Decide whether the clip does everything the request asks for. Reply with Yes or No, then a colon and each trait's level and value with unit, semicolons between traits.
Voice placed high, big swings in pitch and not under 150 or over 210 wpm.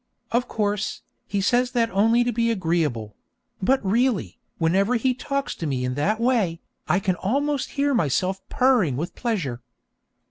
Yes: high, 210 Hz; wide, 6.2 semitones; average, 155 wpm